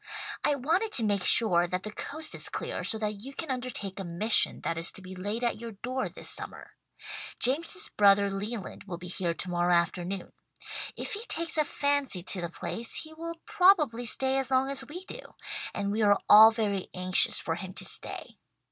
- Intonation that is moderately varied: No, wide, 6.5 semitones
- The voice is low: No, high, 220 Hz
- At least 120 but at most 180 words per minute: No, average, 200 wpm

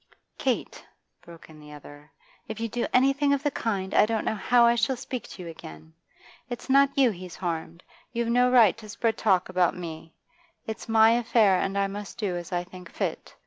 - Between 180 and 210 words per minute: Yes, fast, 205 wpm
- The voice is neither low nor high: No, high, 210 Hz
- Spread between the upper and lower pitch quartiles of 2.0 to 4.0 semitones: No, average, 5.0 semitones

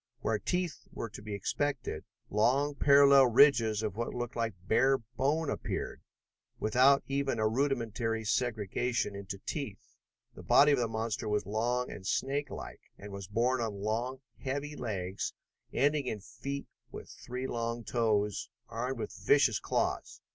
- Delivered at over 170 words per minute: No, average, 145 wpm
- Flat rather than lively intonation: No, average, 4.1 semitones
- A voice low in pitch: Yes, low, 120 Hz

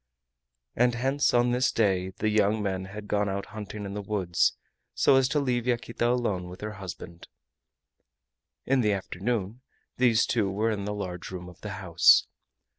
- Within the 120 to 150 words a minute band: No, average, 175 wpm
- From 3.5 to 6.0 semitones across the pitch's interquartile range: Yes, average, 3.9 semitones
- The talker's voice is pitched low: Yes, low, 105 Hz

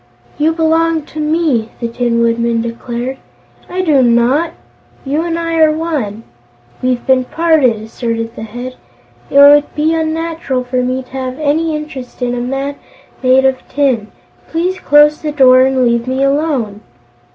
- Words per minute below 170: Yes, average, 160 wpm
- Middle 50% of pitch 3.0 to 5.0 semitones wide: Yes, average, 4.4 semitones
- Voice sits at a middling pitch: No, very high, 265 Hz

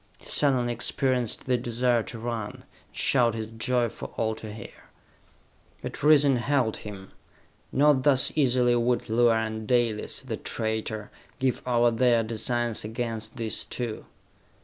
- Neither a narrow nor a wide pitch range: No, narrow, 2.1 semitones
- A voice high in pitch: No, low, 120 Hz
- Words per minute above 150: No, average, 145 wpm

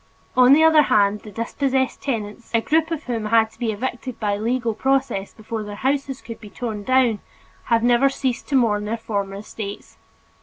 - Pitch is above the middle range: Yes, high, 230 Hz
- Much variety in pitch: No, average, 3.8 semitones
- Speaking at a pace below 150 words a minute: No, average, 190 wpm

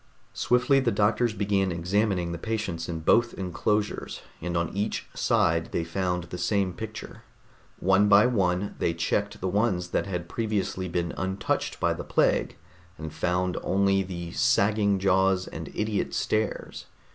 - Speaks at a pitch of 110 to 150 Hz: No, very low, 95 Hz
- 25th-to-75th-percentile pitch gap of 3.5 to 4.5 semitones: No, average, 3.0 semitones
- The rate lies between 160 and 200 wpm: No, average, 150 wpm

